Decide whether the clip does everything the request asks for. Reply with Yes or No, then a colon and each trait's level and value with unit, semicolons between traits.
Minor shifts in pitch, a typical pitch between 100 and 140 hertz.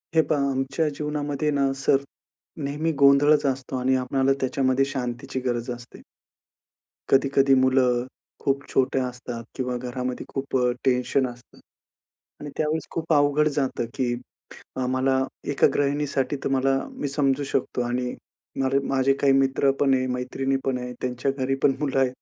Yes: narrow, 1.6 semitones; low, 135 Hz